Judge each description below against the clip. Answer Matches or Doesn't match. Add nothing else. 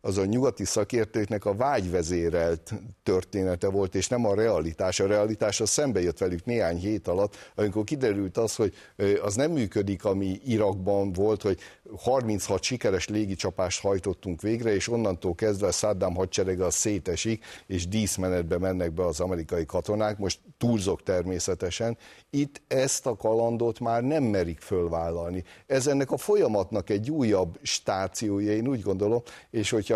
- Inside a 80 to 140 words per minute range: Doesn't match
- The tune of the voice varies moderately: Matches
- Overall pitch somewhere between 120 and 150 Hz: Doesn't match